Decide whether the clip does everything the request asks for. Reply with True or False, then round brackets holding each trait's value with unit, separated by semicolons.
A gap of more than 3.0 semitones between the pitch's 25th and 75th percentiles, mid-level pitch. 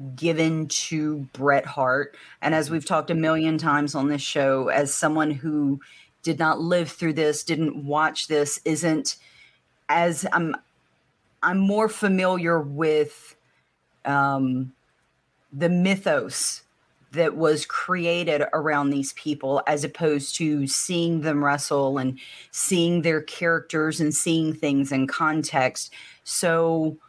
False (2.5 semitones; 155 Hz)